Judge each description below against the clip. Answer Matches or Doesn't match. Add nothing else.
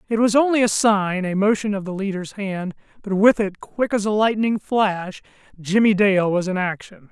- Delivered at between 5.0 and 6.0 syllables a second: Doesn't match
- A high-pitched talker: Matches